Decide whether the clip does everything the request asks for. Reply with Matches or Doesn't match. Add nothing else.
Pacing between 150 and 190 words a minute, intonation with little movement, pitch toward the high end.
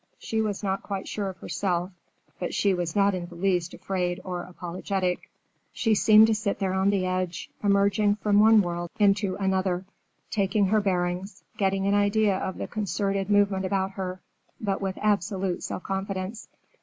Matches